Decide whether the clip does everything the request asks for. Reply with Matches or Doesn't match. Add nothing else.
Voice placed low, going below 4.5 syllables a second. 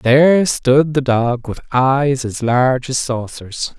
Matches